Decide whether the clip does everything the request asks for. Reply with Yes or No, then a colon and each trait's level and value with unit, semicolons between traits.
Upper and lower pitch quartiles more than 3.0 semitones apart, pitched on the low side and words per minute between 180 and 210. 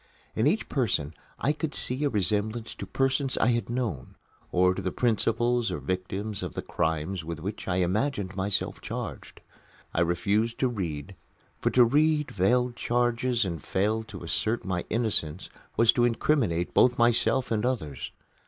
No: average, 4.9 semitones; low, 110 Hz; average, 160 wpm